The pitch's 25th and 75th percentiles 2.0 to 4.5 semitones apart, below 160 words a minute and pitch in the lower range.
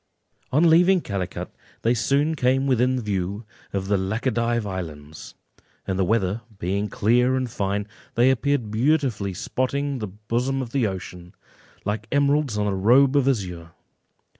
No: average, 5.2 semitones; average, 145 wpm; low, 115 Hz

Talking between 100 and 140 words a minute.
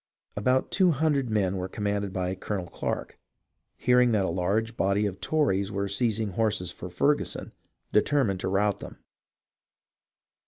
Yes: slow, 135 wpm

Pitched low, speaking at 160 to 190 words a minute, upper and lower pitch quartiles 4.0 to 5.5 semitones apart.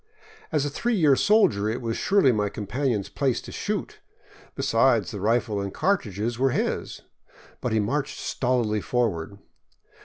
No: low, 120 Hz; average, 150 wpm; average, 4.7 semitones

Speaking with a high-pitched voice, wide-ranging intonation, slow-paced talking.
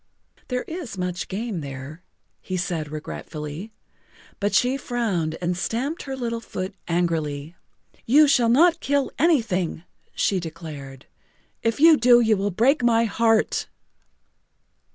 Yes: high, 205 Hz; wide, 6.7 semitones; slow, 130 wpm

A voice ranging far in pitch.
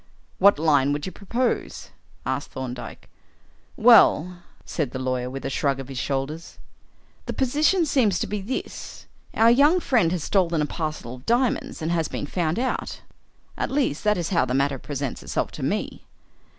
Yes: wide, 7.6 semitones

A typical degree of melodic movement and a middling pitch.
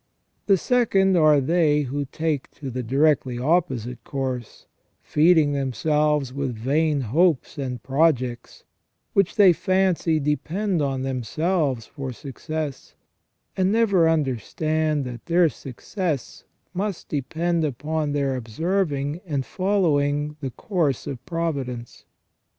Yes: average, 4.1 semitones; medium, 150 Hz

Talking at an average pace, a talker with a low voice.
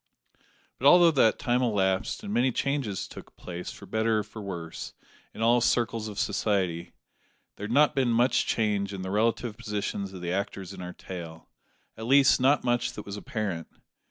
Yes: average, 185 wpm; low, 105 Hz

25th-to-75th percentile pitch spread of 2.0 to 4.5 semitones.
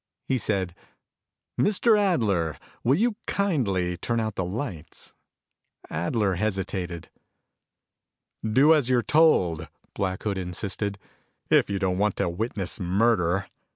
No: average, 5.3 semitones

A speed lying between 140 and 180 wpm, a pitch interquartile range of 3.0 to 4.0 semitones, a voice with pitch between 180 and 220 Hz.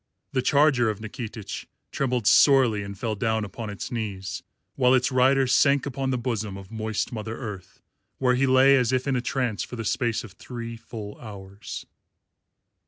No: average, 175 wpm; average, 3.3 semitones; low, 115 Hz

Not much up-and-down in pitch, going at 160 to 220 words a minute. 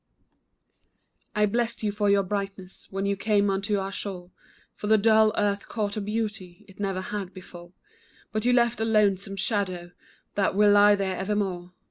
Yes: narrow, 1.6 semitones; average, 170 wpm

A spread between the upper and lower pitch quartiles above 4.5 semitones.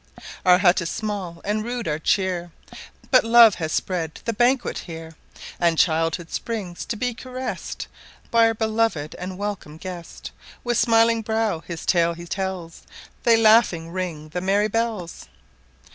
Yes: average, 5.1 semitones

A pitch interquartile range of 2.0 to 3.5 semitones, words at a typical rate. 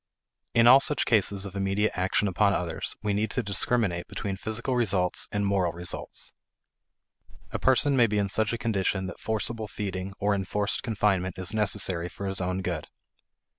Yes: average, 2.7 semitones; average, 170 wpm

